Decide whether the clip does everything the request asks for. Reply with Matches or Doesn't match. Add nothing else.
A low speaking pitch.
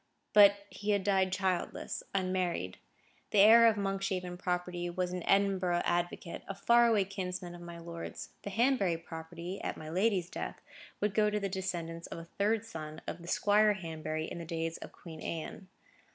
Doesn't match